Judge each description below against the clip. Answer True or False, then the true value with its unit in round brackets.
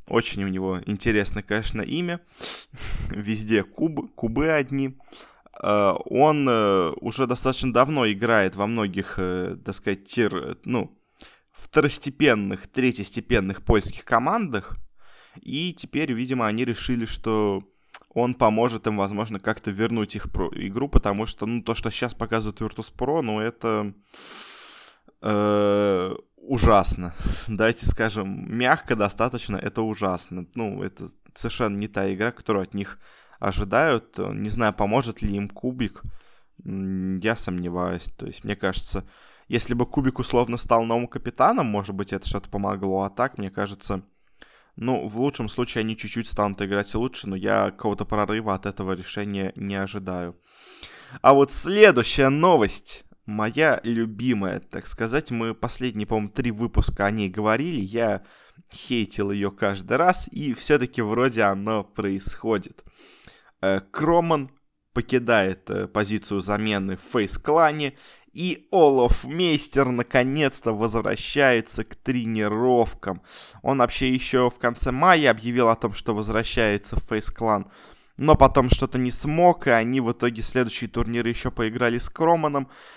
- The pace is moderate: True (130 wpm)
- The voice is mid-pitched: False (110 Hz)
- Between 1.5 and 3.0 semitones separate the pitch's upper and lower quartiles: False (3.7 semitones)